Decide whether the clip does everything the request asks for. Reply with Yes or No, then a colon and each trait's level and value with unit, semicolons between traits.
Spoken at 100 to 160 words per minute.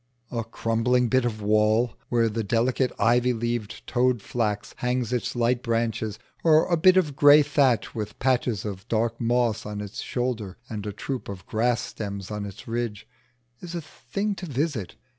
No: average, 175 wpm